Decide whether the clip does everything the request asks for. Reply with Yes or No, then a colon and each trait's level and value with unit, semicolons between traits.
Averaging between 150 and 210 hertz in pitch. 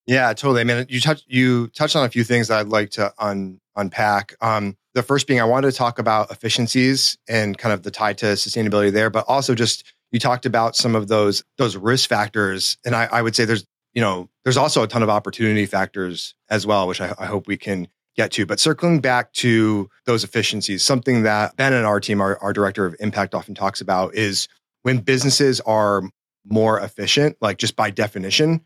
No: low, 110 Hz